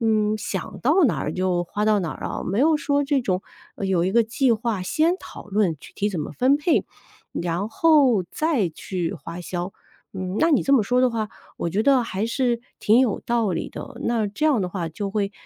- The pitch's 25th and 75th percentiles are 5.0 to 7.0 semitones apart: Yes, wide, 5.5 semitones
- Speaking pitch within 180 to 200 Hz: No, high, 215 Hz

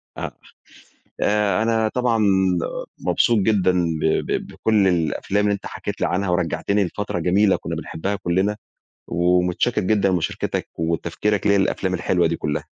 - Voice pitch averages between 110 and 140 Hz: No, very low, 95 Hz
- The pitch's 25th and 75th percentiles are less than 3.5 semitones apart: Yes, average, 2.9 semitones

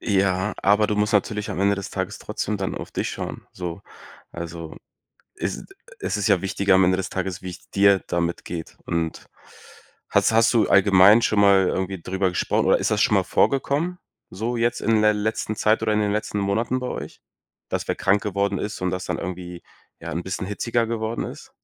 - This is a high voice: No, low, 100 Hz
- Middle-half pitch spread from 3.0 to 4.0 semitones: No, narrow, 2.5 semitones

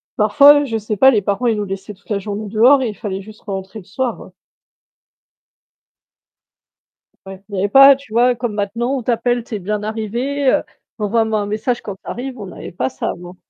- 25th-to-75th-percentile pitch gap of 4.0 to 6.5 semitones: No, average, 3.3 semitones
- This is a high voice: Yes, high, 215 Hz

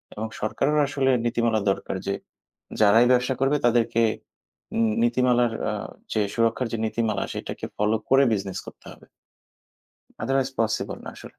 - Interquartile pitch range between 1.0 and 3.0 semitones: Yes, average, 2.7 semitones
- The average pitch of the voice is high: No, low, 115 Hz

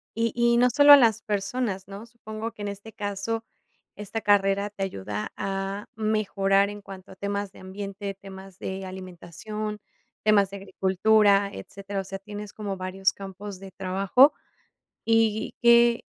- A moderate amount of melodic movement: No, narrow, 1.9 semitones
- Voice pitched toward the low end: No, high, 200 Hz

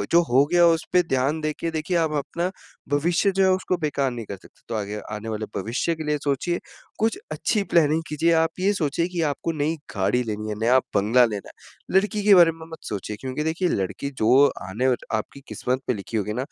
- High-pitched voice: No, medium, 145 Hz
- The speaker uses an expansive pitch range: Yes, wide, 6.3 semitones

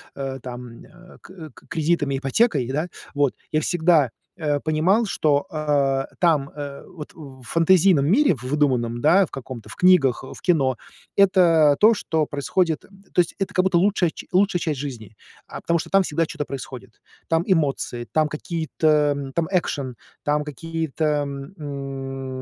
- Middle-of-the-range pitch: Yes, medium, 150 Hz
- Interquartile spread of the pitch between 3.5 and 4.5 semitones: Yes, average, 4.0 semitones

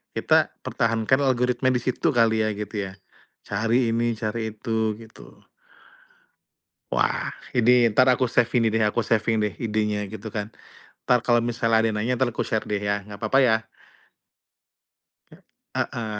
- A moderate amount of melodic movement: No, narrow, 1.9 semitones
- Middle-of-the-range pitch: No, low, 115 Hz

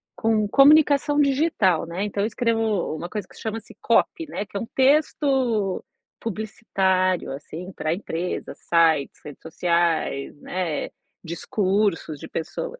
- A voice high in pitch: Yes, high, 200 Hz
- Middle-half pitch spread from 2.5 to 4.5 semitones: No, average, 5.3 semitones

